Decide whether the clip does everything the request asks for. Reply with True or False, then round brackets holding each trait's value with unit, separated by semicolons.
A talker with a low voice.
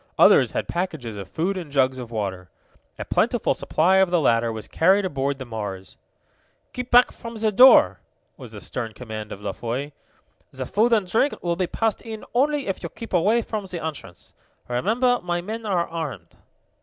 False (170 Hz)